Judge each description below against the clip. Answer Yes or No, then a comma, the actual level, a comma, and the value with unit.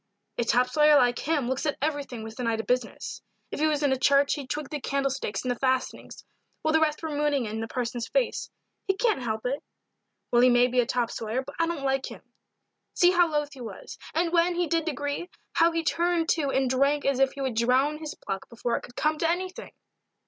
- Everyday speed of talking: No, fast, 235 wpm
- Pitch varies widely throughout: No, average, 3.9 semitones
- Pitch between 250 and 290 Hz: Yes, very high, 275 Hz